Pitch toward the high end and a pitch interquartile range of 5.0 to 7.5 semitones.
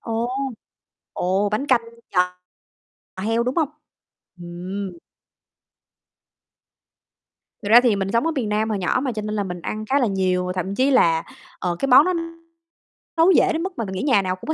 Yes: high, 215 Hz; wide, 5.5 semitones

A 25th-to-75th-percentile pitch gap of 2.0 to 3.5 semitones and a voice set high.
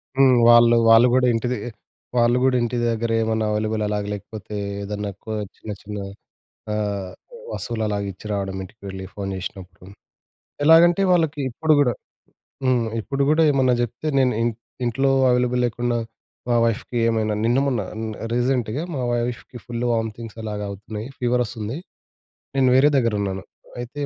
No: average, 2.8 semitones; low, 115 Hz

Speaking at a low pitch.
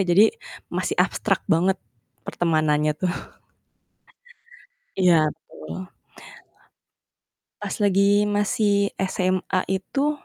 No: medium, 185 Hz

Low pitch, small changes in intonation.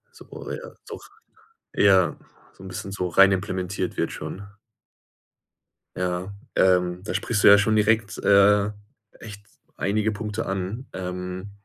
Yes: low, 100 Hz; narrow, 2.1 semitones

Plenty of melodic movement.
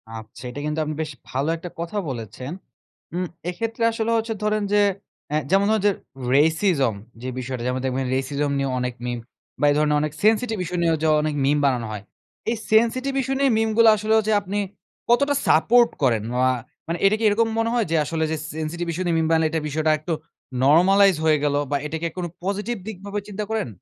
Yes: wide, 6.8 semitones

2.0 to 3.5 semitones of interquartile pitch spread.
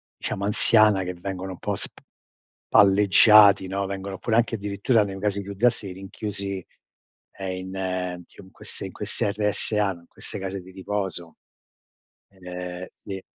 No: narrow, 1.6 semitones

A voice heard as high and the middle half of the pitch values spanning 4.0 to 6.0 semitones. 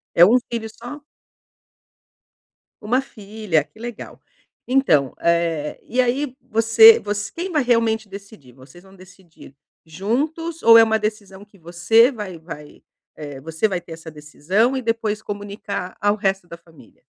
Yes: high, 205 Hz; average, 5.1 semitones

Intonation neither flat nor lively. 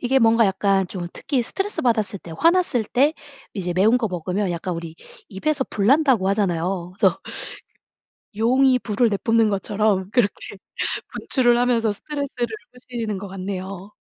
Yes: average, 4.4 semitones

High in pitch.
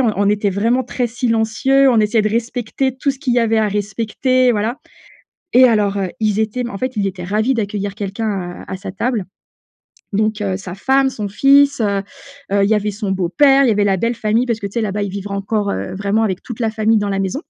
Yes: high, 215 Hz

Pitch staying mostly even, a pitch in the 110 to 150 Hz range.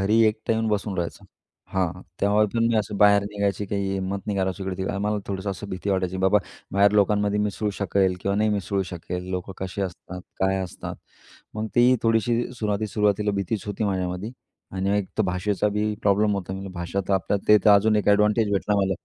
No: narrow, 1.7 semitones; low, 100 Hz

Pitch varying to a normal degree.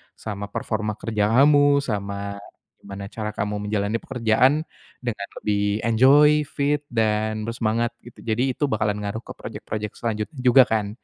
Yes: average, 3.2 semitones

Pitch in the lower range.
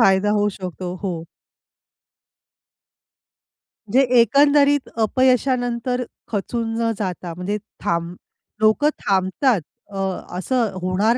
No: high, 215 Hz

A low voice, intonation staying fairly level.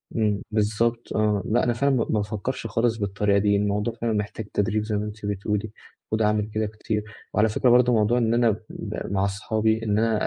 Yes: low, 110 Hz; narrow, 1.7 semitones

